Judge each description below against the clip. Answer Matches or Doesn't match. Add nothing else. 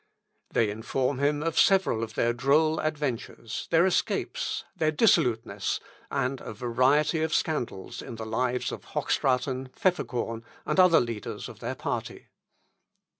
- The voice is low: Matches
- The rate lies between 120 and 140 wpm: Matches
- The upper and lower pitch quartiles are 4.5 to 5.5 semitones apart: Matches